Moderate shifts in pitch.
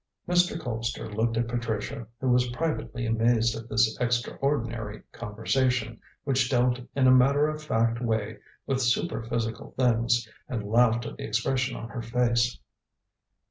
No: narrow, 1.9 semitones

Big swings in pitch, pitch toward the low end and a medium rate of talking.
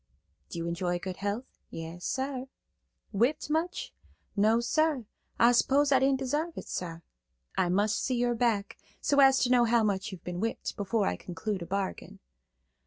No: wide, 5.8 semitones; high, 225 Hz; average, 175 wpm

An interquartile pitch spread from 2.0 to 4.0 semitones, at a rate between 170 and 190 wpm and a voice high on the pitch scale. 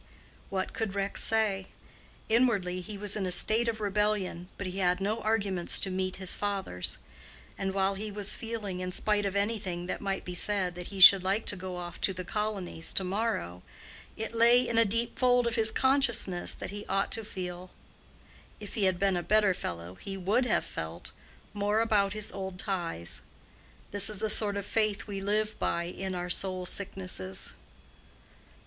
Yes: average, 2.7 semitones; average, 185 wpm; high, 195 Hz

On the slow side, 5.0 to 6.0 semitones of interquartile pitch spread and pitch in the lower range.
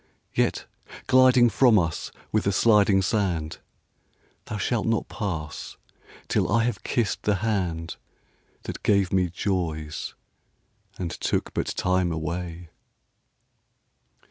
No: slow, 105 wpm; average, 4.2 semitones; very low, 95 Hz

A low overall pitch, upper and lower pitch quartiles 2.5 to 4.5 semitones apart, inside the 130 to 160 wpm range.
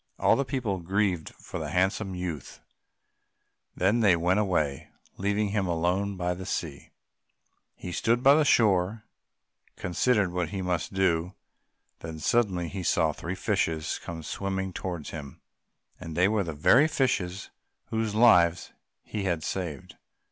Yes: very low, 95 Hz; average, 3.4 semitones; average, 150 wpm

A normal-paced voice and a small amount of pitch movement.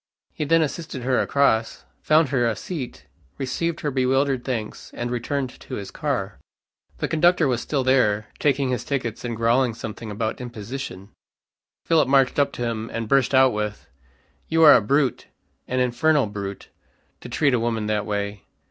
No: average, 170 wpm; average, 3.9 semitones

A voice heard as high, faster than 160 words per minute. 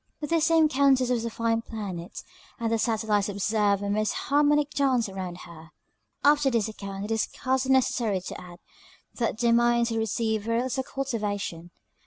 Yes: high, 230 Hz; average, 170 wpm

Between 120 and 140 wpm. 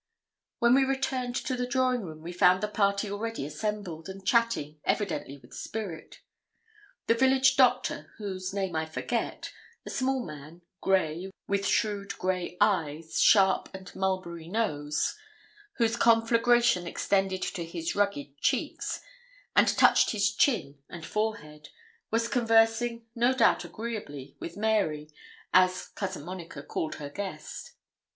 Yes: slow, 135 wpm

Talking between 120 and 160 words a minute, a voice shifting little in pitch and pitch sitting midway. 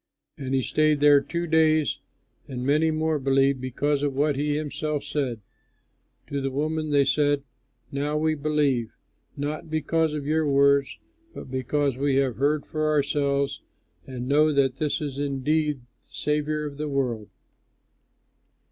Yes: average, 150 wpm; narrow, 1.8 semitones; medium, 145 Hz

